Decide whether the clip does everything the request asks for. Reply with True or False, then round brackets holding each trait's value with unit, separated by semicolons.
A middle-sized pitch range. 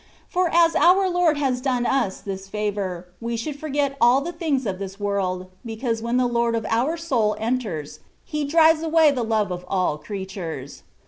False (6.9 semitones)